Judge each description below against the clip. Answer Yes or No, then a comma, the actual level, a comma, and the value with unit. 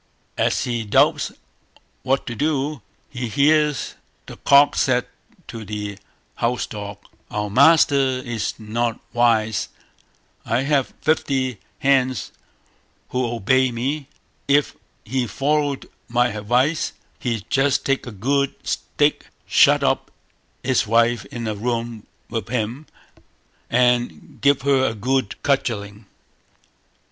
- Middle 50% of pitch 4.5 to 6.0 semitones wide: No, average, 3.3 semitones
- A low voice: Yes, low, 125 Hz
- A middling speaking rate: No, slow, 115 wpm